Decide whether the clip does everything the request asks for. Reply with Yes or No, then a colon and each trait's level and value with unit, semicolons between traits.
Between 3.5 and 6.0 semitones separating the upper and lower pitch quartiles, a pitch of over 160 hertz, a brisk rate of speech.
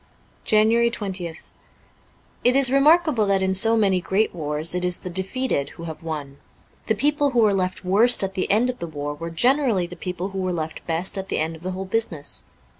Yes: average, 5.1 semitones; high, 190 Hz; fast, 215 wpm